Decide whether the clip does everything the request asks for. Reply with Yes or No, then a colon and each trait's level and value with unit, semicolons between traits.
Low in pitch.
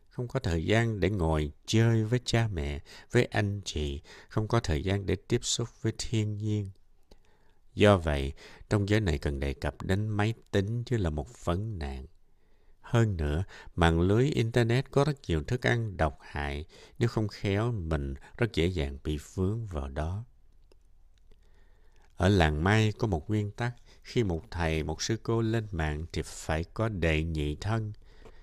Yes: low, 100 Hz